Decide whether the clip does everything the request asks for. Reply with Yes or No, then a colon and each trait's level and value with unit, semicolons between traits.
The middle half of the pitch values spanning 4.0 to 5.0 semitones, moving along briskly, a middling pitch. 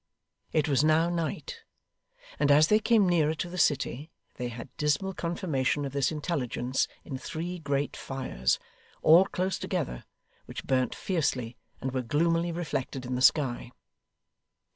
No: average, 4.6 semitones; average, 145 wpm; medium, 150 Hz